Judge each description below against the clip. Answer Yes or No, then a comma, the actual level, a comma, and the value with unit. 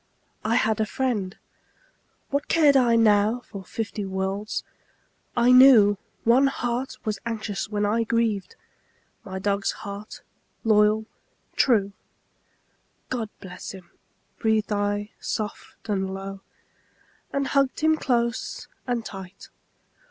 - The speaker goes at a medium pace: No, slow, 115 wpm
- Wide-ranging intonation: No, average, 2.9 semitones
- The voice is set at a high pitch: Yes, high, 215 Hz